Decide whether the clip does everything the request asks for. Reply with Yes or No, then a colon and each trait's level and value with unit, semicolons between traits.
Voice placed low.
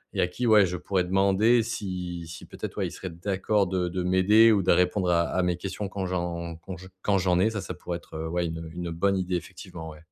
Yes: very low, 90 Hz